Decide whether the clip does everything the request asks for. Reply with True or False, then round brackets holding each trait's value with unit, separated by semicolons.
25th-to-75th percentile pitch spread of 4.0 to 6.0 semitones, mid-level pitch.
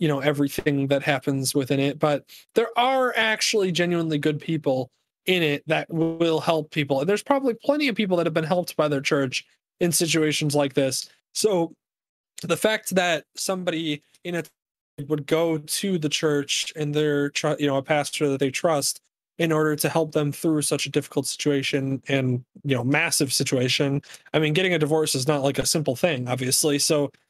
False (2.9 semitones; 150 Hz)